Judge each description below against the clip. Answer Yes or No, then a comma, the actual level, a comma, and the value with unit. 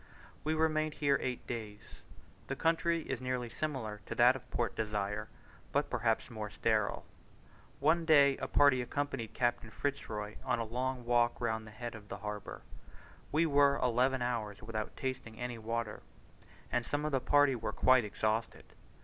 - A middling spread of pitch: Yes, average, 4.2 semitones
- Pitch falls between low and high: No, low, 125 Hz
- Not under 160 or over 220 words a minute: Yes, average, 170 wpm